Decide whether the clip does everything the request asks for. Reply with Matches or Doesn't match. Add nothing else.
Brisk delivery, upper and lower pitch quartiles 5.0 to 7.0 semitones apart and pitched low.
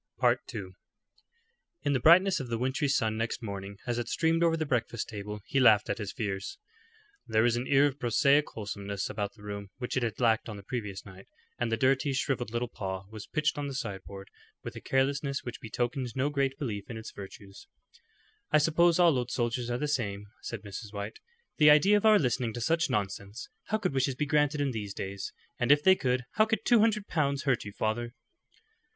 Matches